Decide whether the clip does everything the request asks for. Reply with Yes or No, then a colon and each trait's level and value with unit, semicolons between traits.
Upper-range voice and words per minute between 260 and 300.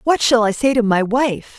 Yes: high, 235 Hz; fast, 265 wpm